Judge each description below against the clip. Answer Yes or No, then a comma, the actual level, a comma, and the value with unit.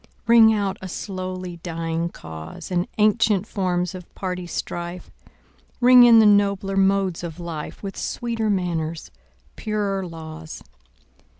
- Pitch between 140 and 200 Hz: Yes, medium, 185 Hz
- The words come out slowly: Yes, slow, 125 wpm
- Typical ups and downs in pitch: Yes, average, 3.2 semitones